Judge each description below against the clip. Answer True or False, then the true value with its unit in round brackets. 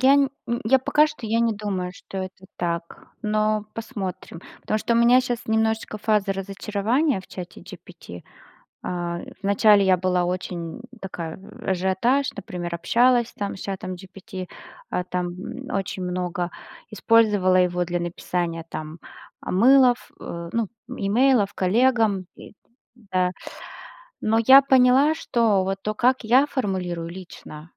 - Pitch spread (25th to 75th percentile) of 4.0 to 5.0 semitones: True (4.4 semitones)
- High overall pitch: True (195 Hz)